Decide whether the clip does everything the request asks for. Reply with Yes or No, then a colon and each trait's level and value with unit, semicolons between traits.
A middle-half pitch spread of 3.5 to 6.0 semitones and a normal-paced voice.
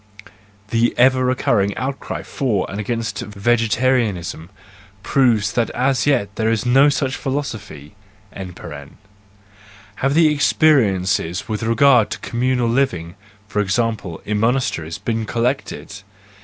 No: average, 4.4 semitones; slow, 115 wpm